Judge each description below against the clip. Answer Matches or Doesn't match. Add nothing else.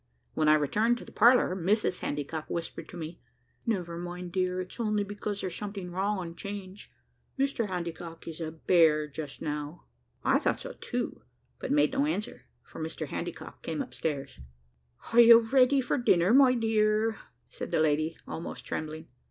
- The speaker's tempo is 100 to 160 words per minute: Doesn't match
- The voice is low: Doesn't match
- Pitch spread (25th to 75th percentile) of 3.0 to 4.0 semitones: Doesn't match